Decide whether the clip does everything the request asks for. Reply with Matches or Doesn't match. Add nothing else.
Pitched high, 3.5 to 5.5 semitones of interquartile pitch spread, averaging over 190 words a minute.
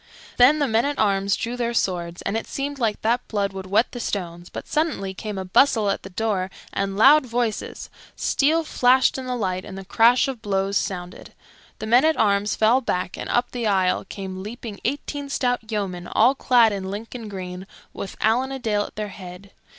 Matches